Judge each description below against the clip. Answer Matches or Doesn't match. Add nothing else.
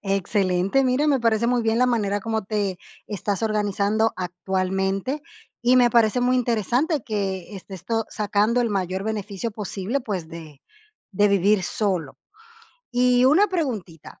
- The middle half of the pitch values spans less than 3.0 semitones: Doesn't match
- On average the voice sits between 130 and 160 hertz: Doesn't match